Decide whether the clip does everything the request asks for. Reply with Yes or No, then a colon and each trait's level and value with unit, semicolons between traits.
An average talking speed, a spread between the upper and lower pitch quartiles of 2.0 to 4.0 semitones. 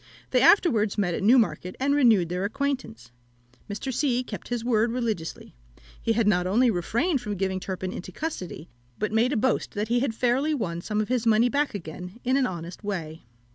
No: average, 190 wpm; average, 5.2 semitones